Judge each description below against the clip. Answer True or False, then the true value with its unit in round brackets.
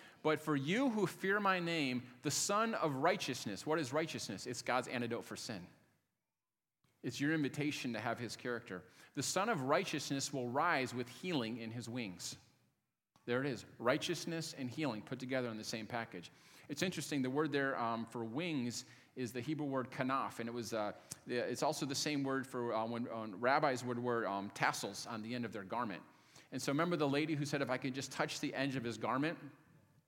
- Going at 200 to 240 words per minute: True (205 wpm)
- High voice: False (130 Hz)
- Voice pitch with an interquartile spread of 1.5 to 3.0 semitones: False (4.2 semitones)